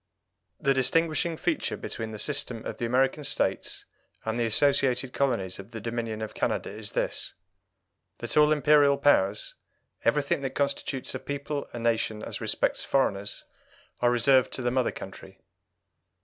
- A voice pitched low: Yes, low, 125 Hz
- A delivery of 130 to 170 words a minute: Yes, average, 150 wpm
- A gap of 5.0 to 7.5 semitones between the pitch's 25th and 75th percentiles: No, average, 3.9 semitones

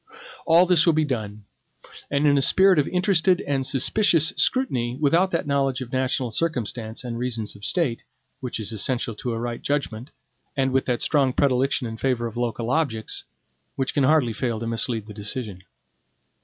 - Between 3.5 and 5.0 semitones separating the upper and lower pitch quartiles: Yes, average, 4.2 semitones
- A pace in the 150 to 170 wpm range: No, average, 180 wpm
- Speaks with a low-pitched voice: Yes, low, 130 Hz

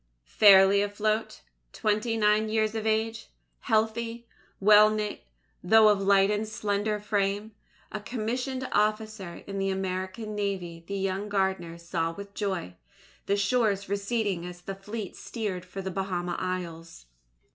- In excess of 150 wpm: No, slow, 135 wpm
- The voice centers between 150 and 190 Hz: No, high, 205 Hz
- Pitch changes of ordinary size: No, narrow, 2.2 semitones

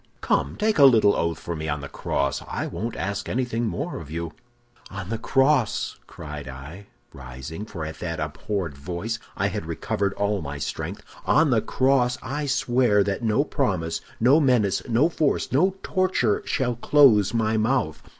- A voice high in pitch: No, low, 105 Hz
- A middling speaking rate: Yes, average, 170 wpm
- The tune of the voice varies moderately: No, wide, 7.4 semitones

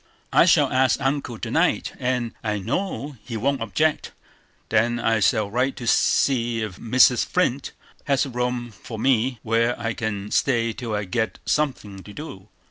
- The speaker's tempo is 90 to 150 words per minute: No, average, 170 wpm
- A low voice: Yes, low, 120 Hz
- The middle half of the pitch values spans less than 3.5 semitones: Yes, average, 3.1 semitones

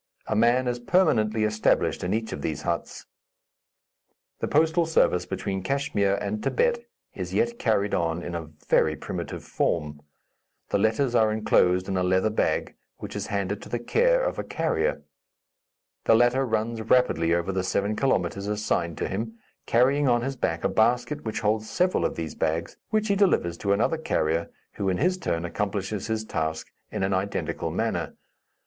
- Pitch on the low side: Yes, low, 110 Hz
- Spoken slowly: No, average, 175 wpm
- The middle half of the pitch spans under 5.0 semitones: No, average, 5.3 semitones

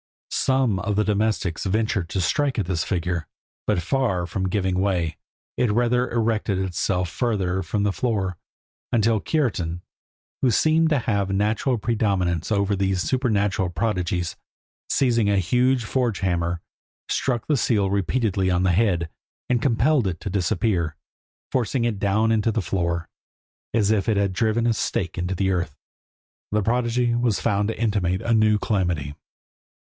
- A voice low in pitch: Yes, low, 100 Hz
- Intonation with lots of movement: No, average, 4.0 semitones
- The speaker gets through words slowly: No, average, 155 wpm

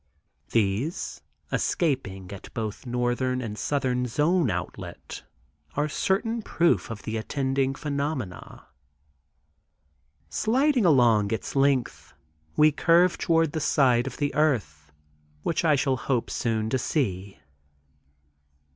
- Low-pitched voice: Yes, low, 130 Hz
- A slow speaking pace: Yes, slow, 110 wpm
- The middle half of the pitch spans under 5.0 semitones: No, average, 5.3 semitones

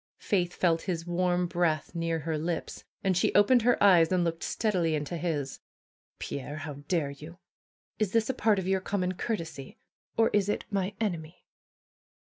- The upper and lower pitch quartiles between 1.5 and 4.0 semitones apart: Yes, average, 3.3 semitones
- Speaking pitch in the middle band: Yes, medium, 175 Hz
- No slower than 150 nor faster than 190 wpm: Yes, average, 170 wpm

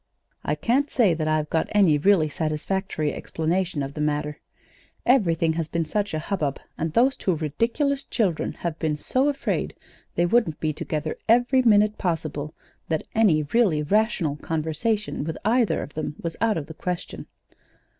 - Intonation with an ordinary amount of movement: No, wide, 5.9 semitones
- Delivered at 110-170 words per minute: Yes, average, 165 wpm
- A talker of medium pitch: Yes, medium, 165 Hz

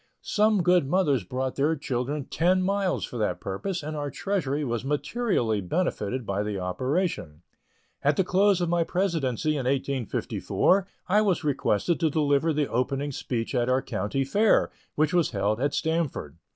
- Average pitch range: No, wide, 6.0 semitones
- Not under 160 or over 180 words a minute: Yes, average, 165 wpm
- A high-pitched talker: No, medium, 145 Hz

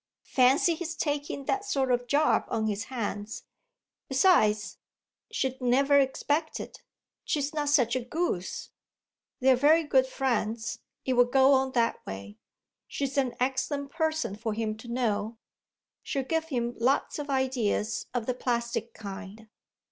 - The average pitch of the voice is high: Yes, very high, 255 Hz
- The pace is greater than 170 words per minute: No, average, 145 wpm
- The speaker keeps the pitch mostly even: No, average, 3.8 semitones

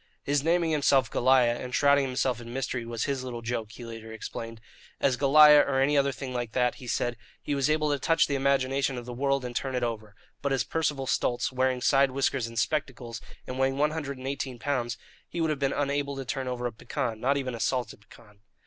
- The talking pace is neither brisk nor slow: No, fast, 230 wpm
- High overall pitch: No, low, 130 Hz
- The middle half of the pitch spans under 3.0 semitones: Yes, narrow, 2.6 semitones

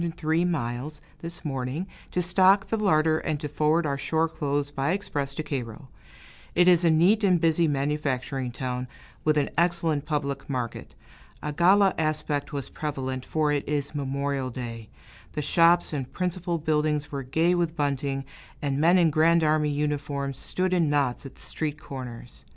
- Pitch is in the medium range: Yes, medium, 150 Hz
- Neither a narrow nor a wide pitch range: Yes, average, 3.3 semitones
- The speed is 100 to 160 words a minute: No, average, 170 wpm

